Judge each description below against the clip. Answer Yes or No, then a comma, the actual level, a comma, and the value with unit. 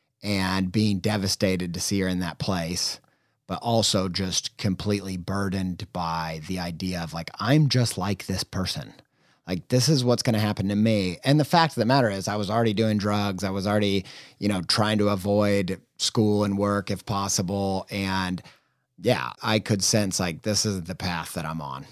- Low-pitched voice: Yes, low, 100 Hz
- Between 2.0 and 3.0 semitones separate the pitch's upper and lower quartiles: Yes, narrow, 2.4 semitones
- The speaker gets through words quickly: No, average, 190 wpm